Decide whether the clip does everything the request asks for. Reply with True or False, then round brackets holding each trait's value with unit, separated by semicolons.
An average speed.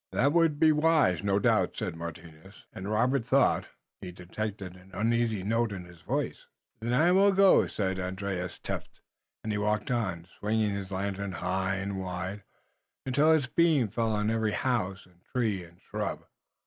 True (170 wpm)